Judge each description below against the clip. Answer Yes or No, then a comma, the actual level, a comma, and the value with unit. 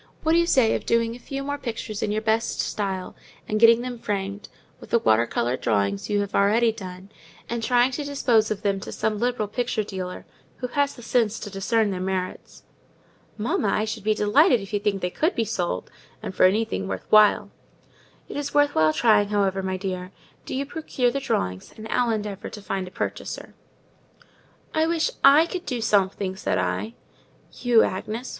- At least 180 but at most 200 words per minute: Yes, average, 195 wpm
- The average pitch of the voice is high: Yes, high, 215 Hz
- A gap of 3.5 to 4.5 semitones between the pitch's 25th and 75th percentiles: Yes, average, 4.0 semitones